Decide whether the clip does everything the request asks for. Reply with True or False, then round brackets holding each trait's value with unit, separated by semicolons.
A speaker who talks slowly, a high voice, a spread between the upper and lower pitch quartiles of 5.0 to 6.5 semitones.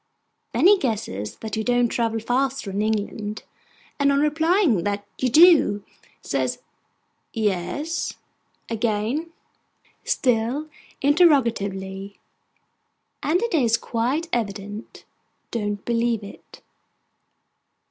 True (100 wpm; 230 Hz; 5.5 semitones)